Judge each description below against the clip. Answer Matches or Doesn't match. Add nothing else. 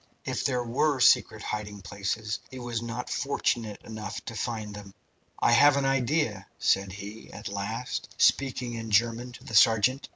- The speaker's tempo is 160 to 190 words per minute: Matches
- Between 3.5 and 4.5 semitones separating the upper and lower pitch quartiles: Doesn't match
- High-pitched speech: Doesn't match